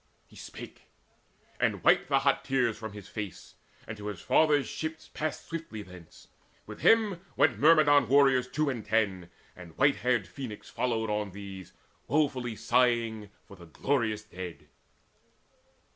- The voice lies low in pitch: Yes, low, 115 Hz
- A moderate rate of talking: Yes, average, 150 wpm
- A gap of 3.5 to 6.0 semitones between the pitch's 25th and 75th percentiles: Yes, average, 5.1 semitones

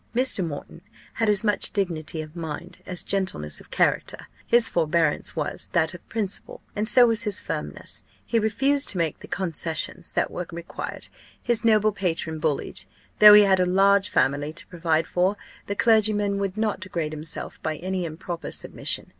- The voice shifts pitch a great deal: No, average, 4.3 semitones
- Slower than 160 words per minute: No, average, 170 wpm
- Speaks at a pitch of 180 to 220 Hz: Yes, medium, 185 Hz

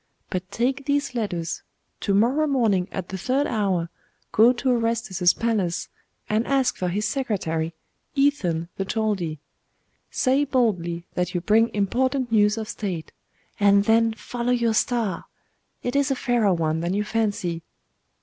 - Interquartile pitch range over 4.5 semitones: Yes, average, 5.2 semitones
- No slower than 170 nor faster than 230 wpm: No, average, 150 wpm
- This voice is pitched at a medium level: No, high, 215 Hz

